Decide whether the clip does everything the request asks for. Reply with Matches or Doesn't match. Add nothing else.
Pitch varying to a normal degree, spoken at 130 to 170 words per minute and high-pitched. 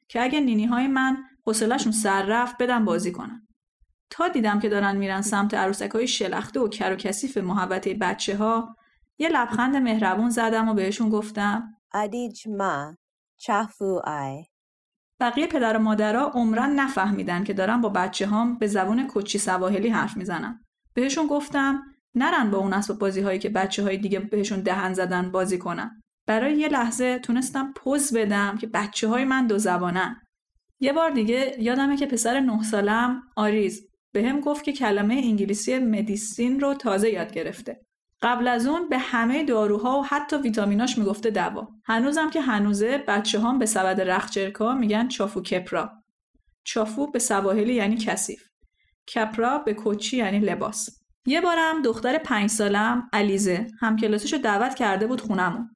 Matches